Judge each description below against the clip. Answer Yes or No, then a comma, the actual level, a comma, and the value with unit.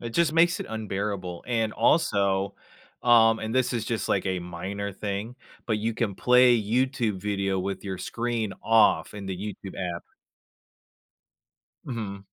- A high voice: No, low, 105 Hz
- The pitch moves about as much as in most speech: Yes, average, 3.2 semitones